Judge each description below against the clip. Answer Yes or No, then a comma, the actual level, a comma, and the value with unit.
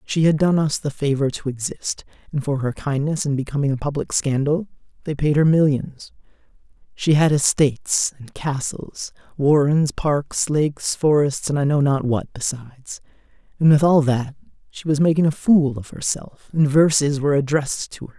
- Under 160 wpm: No, average, 175 wpm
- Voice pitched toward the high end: No, medium, 145 Hz